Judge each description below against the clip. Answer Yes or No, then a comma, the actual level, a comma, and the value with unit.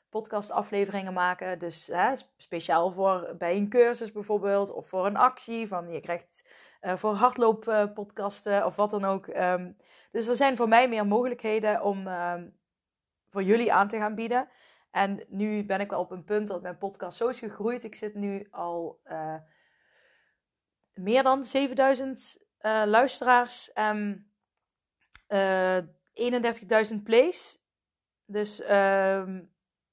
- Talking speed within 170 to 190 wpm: No, average, 145 wpm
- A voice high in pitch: Yes, high, 210 Hz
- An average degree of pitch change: Yes, average, 3.4 semitones